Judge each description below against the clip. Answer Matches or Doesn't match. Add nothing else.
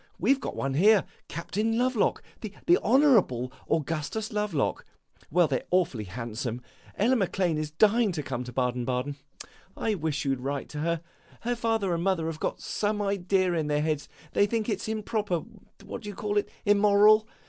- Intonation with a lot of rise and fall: Matches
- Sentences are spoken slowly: Doesn't match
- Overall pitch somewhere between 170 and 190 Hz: Matches